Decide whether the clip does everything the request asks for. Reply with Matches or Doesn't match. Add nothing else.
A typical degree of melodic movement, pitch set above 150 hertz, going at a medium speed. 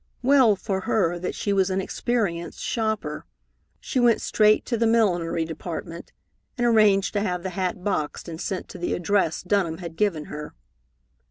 Matches